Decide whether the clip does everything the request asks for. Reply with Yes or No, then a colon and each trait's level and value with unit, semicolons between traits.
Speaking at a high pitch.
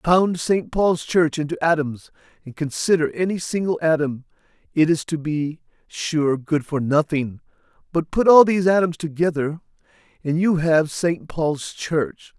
No: medium, 160 Hz